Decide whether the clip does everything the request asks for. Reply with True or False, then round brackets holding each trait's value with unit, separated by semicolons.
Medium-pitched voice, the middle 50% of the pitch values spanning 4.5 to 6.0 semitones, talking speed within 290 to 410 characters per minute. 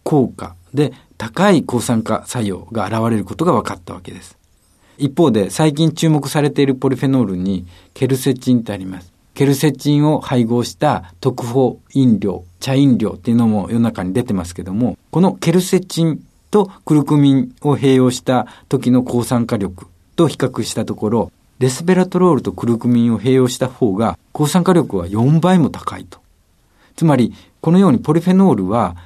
False (125 Hz; 5.6 semitones; 355 characters per minute)